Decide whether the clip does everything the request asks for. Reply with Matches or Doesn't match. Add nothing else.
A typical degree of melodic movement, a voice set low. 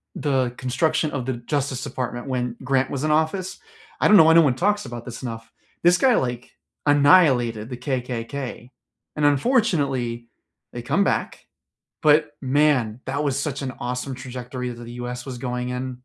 Matches